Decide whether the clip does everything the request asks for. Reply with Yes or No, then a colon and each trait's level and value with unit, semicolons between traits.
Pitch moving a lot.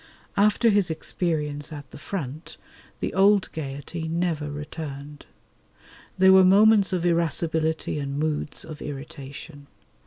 No: average, 3.9 semitones